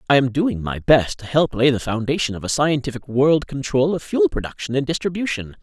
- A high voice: No, low, 135 Hz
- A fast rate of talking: Yes, fast, 215 wpm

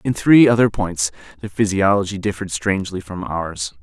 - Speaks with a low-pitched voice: Yes, very low, 95 Hz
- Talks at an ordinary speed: Yes, average, 155 wpm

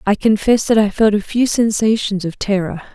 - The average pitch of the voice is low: No, high, 210 Hz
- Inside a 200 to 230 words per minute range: Yes, fast, 205 wpm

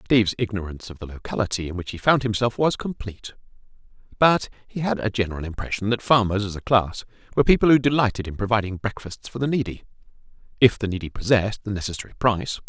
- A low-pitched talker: Yes, low, 110 Hz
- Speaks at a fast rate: No, average, 190 wpm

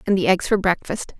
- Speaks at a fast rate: Yes, fast, 250 wpm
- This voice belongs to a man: No, female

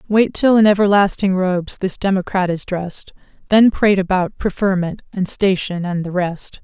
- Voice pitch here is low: No, high, 190 Hz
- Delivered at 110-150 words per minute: No, average, 165 wpm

